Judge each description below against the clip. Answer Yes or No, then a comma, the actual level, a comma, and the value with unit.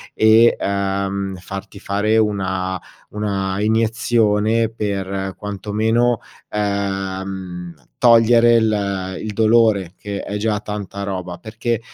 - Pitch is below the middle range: Yes, low, 100 Hz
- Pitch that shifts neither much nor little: No, narrow, 2.3 semitones